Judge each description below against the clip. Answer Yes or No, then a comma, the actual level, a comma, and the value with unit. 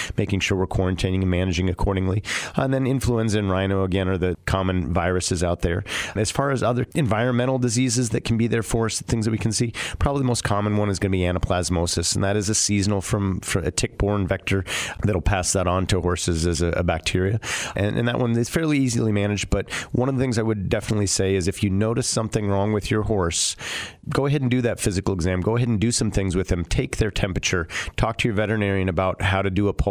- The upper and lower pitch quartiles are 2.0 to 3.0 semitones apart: No, average, 3.6 semitones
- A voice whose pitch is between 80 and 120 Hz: Yes, low, 100 Hz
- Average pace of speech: No, fast, 245 wpm